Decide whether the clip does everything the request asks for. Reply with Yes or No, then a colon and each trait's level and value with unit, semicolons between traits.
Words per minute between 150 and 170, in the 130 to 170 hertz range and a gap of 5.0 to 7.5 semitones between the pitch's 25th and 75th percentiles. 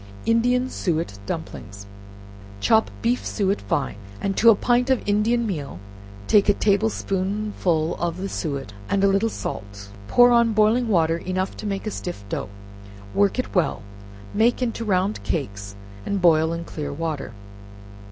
No: average, 155 wpm; high, 195 Hz; wide, 5.6 semitones